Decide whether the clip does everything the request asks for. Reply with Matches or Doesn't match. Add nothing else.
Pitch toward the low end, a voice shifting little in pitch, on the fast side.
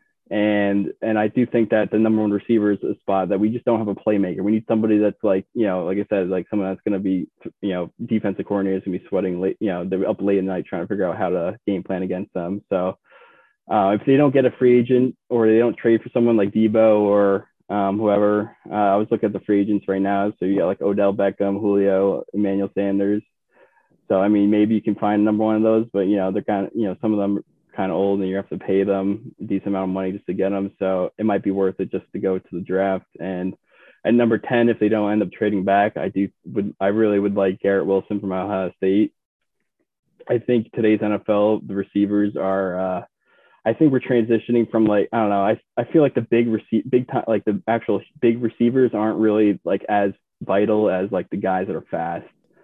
Matches